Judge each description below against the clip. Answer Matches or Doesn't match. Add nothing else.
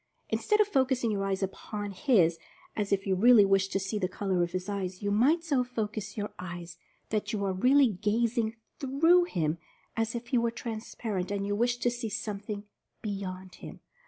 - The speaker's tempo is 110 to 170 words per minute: Doesn't match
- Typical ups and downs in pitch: Matches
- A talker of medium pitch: Doesn't match